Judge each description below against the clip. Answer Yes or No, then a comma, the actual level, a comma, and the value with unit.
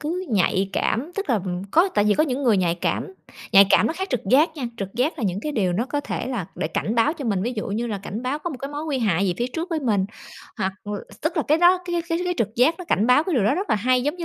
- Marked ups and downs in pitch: Yes, wide, 7.4 semitones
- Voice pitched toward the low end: No, very high, 250 Hz